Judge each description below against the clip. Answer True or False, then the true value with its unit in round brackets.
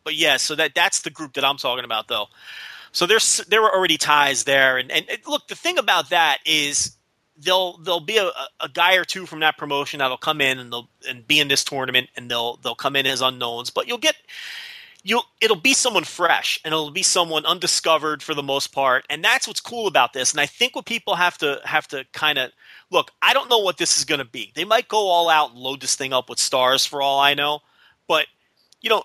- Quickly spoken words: True (245 wpm)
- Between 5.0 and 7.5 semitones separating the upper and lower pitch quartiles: True (5.6 semitones)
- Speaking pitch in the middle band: True (150 Hz)